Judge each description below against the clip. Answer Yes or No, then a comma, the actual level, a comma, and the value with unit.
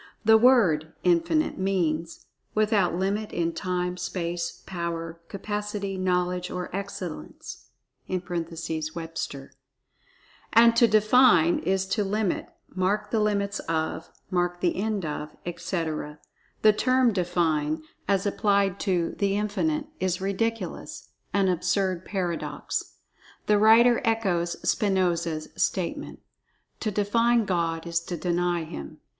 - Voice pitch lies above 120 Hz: Yes, medium, 185 Hz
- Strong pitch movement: No, average, 3.5 semitones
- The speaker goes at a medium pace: No, slow, 115 wpm